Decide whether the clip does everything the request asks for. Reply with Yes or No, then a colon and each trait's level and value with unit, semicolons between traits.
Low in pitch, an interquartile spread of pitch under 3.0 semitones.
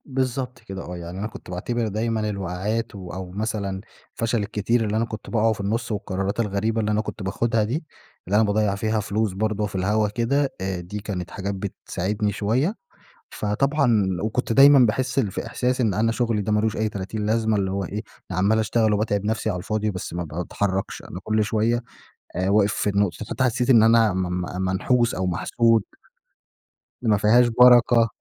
Yes: low, 105 Hz; narrow, 2.6 semitones